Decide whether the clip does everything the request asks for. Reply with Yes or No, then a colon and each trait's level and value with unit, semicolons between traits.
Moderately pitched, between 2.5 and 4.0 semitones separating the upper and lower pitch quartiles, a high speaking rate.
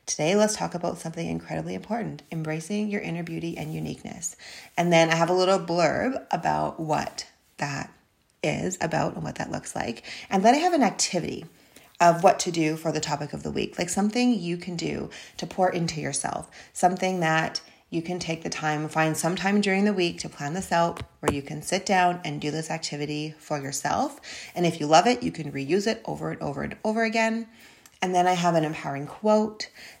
Yes: medium, 170 Hz; average, 3.7 semitones; fast, 210 wpm